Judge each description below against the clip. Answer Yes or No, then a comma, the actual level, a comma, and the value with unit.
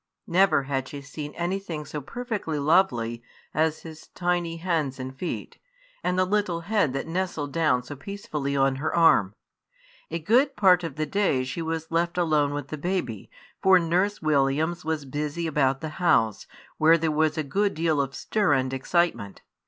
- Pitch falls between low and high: Yes, medium, 160 Hz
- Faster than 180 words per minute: No, average, 175 wpm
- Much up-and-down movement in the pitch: No, average, 4.0 semitones